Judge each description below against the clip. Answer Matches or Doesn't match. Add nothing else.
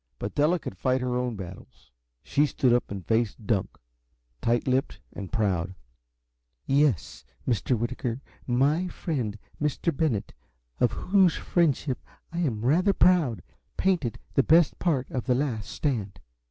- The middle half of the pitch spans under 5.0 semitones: Doesn't match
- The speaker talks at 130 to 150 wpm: Matches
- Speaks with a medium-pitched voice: Doesn't match